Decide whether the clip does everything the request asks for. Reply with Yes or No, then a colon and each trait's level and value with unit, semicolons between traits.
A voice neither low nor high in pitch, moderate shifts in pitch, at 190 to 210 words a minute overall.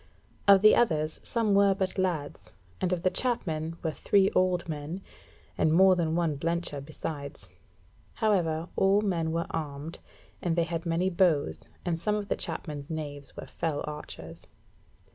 No: medium, 165 Hz; average, 3.4 semitones; average, 160 wpm